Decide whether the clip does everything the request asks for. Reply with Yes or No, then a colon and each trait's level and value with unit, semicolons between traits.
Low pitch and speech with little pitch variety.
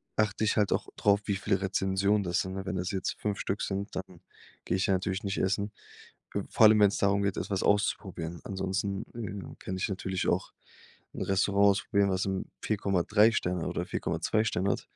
Yes: low, 100 Hz; narrow, 1.3 semitones